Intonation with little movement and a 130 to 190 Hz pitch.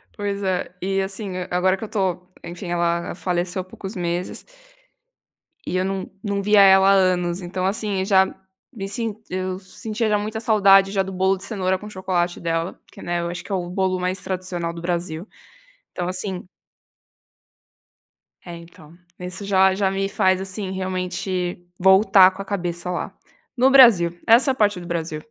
Yes: narrow, 1.8 semitones; medium, 185 Hz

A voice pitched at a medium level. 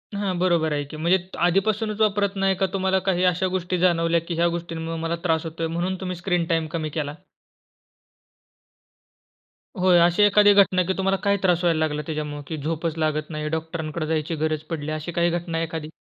Yes: medium, 170 Hz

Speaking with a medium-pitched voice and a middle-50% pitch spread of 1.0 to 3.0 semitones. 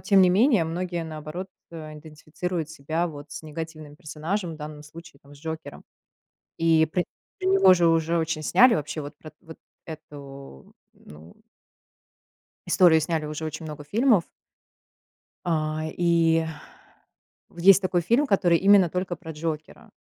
Yes: medium, 160 Hz; narrow, 2.5 semitones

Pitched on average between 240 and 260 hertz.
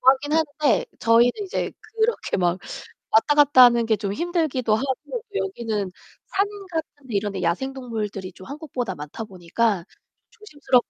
Yes: high, 245 Hz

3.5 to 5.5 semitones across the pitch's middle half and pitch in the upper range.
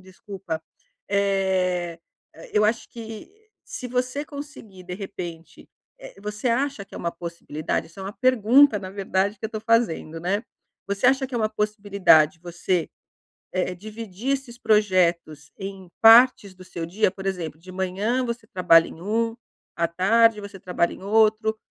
Yes: average, 3.8 semitones; high, 200 Hz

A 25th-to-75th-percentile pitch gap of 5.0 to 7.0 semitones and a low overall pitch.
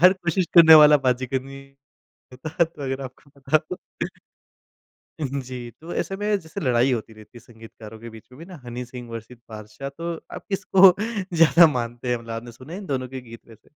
Yes: average, 5.3 semitones; low, 130 Hz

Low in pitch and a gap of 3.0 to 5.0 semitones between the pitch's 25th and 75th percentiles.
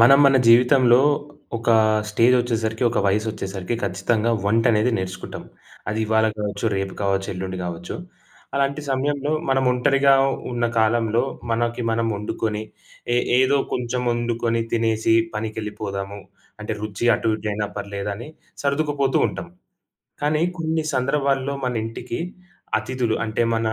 Yes: low, 115 Hz; average, 3.5 semitones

